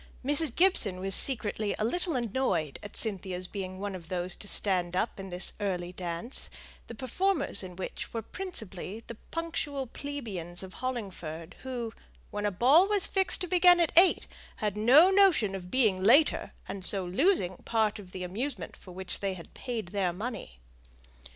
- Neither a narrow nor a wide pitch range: No, wide, 6.5 semitones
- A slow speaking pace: No, average, 170 wpm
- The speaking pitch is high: Yes, high, 210 Hz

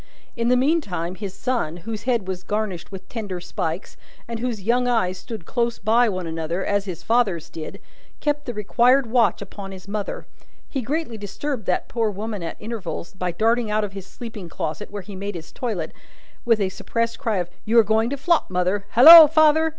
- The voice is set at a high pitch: Yes, high, 215 Hz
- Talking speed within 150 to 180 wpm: No, average, 195 wpm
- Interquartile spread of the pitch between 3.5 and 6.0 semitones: Yes, average, 4.2 semitones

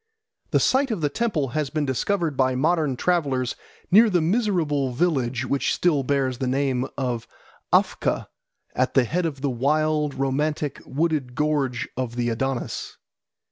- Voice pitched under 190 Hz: Yes, medium, 140 Hz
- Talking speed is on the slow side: No, average, 150 wpm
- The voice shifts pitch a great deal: No, average, 3.5 semitones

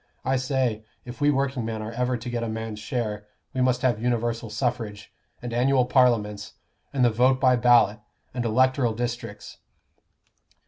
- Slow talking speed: No, average, 155 wpm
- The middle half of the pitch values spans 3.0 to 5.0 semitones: No, narrow, 2.4 semitones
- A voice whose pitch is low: Yes, low, 120 Hz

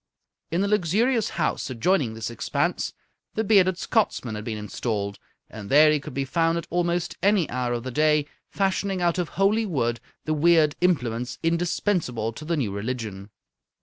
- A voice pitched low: No, medium, 155 Hz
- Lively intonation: Yes, wide, 7.2 semitones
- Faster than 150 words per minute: Yes, average, 170 wpm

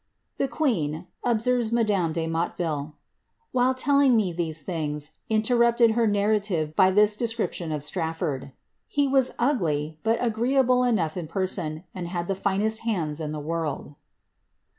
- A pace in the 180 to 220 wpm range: No, average, 160 wpm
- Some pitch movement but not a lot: No, wide, 6.7 semitones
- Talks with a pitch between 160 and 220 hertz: Yes, high, 190 Hz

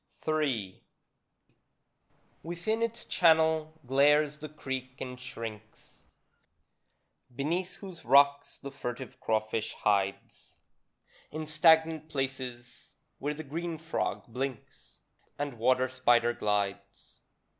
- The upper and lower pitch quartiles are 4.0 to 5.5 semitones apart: Yes, average, 4.6 semitones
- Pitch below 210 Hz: Yes, medium, 140 Hz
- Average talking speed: No, slow, 95 wpm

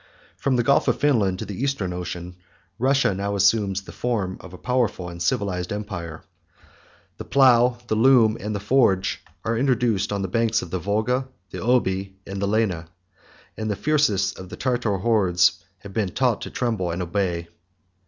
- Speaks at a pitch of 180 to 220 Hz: No, low, 100 Hz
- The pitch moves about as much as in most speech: Yes, average, 4.4 semitones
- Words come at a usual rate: Yes, average, 180 wpm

